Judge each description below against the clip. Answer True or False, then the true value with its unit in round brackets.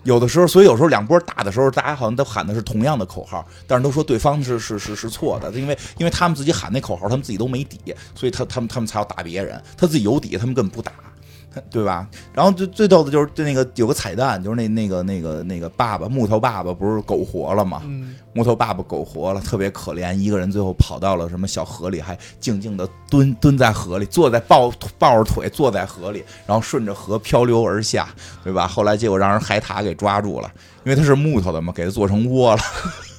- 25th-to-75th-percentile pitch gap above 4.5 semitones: True (5.2 semitones)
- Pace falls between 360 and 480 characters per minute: True (365 characters per minute)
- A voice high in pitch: False (110 Hz)